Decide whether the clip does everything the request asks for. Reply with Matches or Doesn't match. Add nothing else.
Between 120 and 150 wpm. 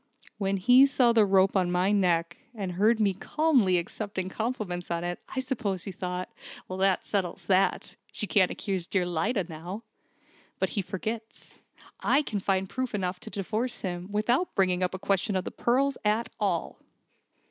Doesn't match